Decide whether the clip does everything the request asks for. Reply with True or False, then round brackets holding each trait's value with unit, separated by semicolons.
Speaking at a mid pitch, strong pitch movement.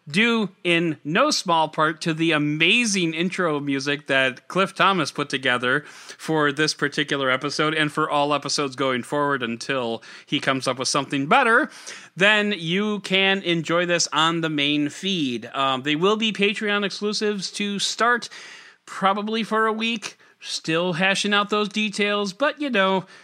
True (170 Hz; 5.8 semitones)